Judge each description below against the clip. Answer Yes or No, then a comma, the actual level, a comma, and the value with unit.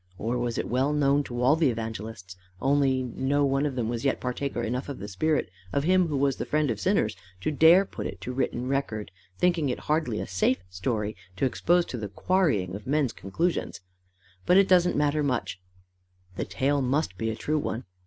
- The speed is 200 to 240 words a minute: Yes, fast, 205 wpm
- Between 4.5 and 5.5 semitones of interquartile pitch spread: Yes, average, 4.9 semitones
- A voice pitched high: No, low, 130 Hz